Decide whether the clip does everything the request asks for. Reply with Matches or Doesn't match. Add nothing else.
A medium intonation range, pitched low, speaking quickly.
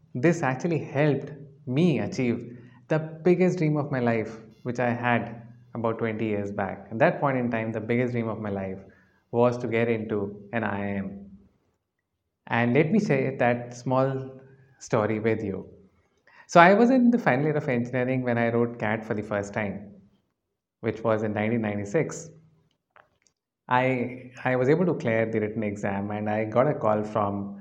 Doesn't match